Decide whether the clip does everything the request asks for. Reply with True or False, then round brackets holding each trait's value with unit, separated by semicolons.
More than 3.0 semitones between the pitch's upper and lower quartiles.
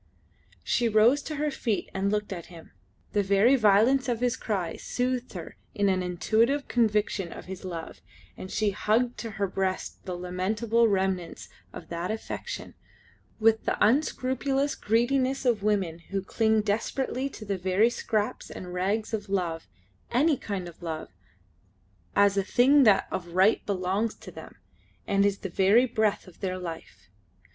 True (4.0 semitones)